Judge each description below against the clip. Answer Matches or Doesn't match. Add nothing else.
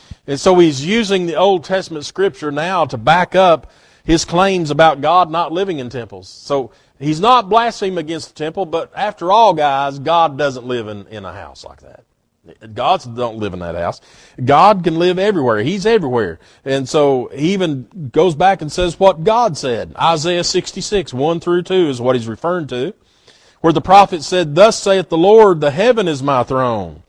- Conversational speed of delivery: Matches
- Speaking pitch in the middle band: Matches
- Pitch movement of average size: Doesn't match